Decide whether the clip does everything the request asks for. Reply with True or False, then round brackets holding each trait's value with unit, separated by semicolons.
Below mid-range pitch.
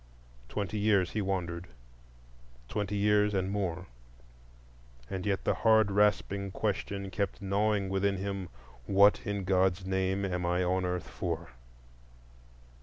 True (95 Hz)